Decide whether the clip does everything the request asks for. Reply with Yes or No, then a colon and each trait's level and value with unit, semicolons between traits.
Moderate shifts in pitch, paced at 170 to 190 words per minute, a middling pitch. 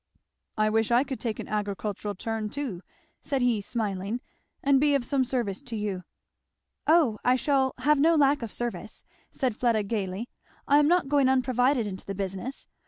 No: average, 4.6 semitones; average, 175 wpm; high, 240 Hz